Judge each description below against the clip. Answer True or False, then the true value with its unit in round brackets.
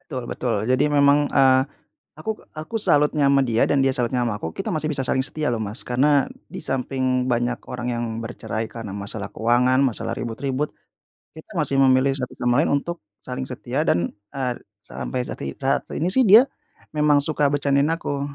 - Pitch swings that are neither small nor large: True (3.0 semitones)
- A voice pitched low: True (130 Hz)